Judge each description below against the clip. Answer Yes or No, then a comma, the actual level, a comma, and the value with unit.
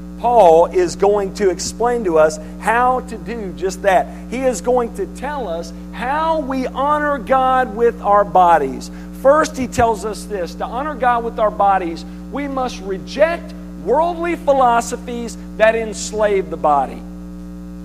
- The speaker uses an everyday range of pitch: No, wide, 6.9 semitones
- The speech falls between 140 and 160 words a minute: Yes, average, 150 wpm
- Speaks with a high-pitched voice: Yes, high, 205 Hz